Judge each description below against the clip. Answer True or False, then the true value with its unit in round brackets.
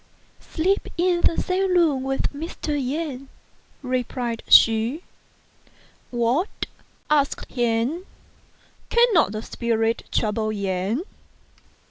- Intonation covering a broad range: True (6.4 semitones)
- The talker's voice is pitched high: True (265 Hz)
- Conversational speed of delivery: False (105 wpm)